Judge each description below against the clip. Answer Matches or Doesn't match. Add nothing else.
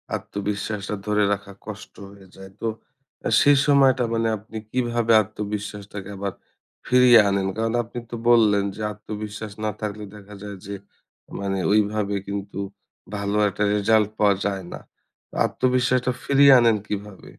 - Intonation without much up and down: Matches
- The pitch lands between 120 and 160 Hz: Doesn't match